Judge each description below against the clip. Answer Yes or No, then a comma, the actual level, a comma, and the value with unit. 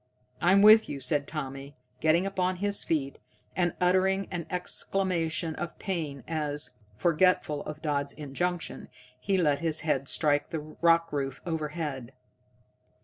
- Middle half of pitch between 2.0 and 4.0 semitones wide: Yes, average, 3.7 semitones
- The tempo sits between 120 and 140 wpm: Yes, slow, 135 wpm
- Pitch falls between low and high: Yes, medium, 160 Hz